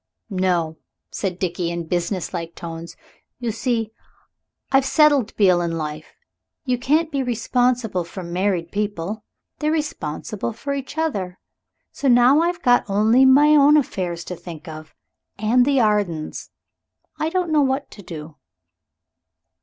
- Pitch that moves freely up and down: Yes, wide, 7.6 semitones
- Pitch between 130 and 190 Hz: No, high, 210 Hz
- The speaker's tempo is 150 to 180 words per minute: No, average, 140 wpm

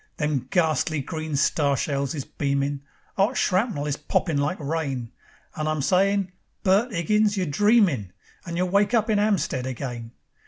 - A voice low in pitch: No, medium, 155 Hz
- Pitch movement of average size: No, wide, 5.9 semitones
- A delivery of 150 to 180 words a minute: Yes, average, 155 wpm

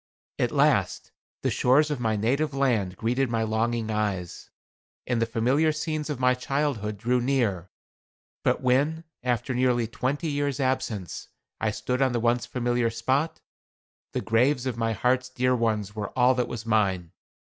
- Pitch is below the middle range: Yes, low, 125 Hz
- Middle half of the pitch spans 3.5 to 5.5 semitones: No, average, 2.9 semitones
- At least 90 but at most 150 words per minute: No, average, 160 wpm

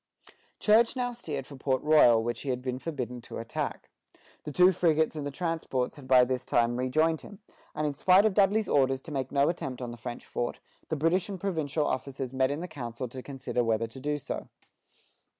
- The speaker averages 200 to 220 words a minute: Yes, fast, 205 wpm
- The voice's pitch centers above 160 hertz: No, medium, 140 Hz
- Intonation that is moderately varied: Yes, average, 4.4 semitones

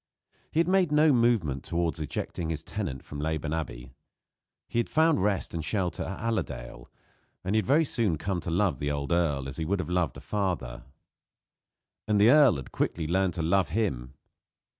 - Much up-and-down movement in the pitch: Yes, wide, 5.9 semitones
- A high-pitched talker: No, very low, 90 Hz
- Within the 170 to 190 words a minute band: Yes, average, 185 wpm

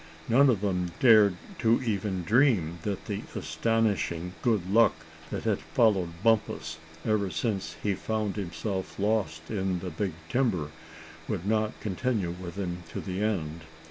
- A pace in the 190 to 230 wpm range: No, average, 145 wpm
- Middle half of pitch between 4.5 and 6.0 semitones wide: No, average, 3.7 semitones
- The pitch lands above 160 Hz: No, low, 100 Hz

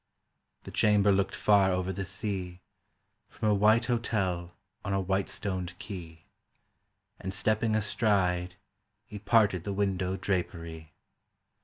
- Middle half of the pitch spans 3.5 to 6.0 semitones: No, narrow, 2.5 semitones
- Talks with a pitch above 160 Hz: No, very low, 95 Hz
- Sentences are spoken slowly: Yes, slow, 130 wpm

